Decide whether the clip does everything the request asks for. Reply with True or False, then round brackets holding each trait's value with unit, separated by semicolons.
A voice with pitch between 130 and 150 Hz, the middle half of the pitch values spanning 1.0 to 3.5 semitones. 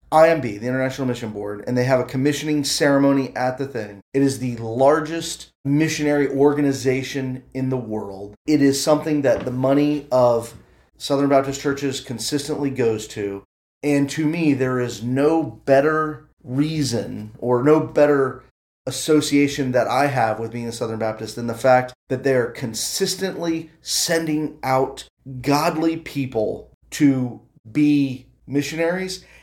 True (135 Hz; 3.1 semitones)